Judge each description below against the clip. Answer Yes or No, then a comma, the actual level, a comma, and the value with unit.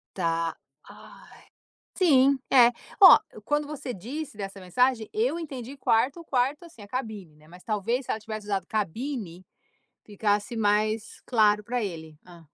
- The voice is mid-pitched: No, high, 220 Hz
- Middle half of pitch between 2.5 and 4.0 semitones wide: No, average, 4.9 semitones